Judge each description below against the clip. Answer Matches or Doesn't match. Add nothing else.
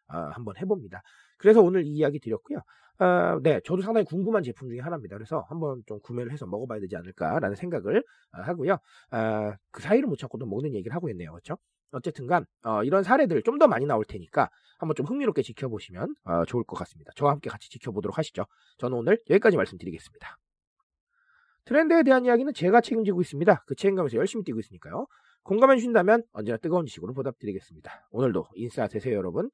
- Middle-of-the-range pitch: Matches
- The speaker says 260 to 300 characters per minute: Doesn't match